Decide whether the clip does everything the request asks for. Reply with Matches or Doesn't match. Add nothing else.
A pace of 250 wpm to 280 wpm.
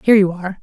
Doesn't match